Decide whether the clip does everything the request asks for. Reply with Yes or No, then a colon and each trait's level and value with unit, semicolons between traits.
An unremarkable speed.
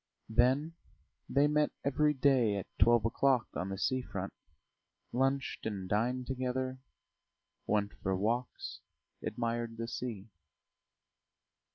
No: slow, 110 wpm